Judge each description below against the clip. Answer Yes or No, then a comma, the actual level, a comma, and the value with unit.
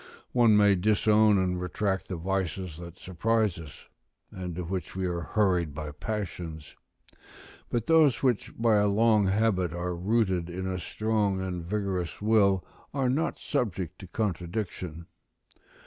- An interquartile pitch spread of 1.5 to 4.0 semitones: Yes, average, 3.5 semitones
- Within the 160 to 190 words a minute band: No, average, 145 wpm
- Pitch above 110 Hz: No, very low, 95 Hz